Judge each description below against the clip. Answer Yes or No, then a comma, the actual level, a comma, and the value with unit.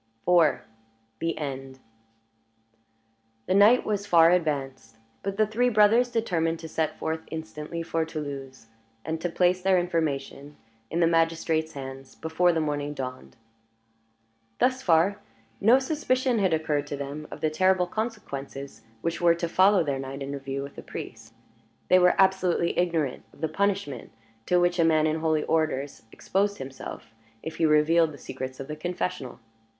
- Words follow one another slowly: No, average, 155 wpm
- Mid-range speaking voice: Yes, medium, 160 Hz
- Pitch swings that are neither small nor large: Yes, average, 4.2 semitones